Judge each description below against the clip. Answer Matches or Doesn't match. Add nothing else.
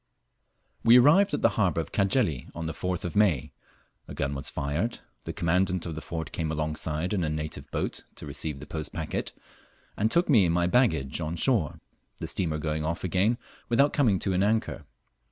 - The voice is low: Matches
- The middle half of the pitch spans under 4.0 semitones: Doesn't match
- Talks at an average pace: Matches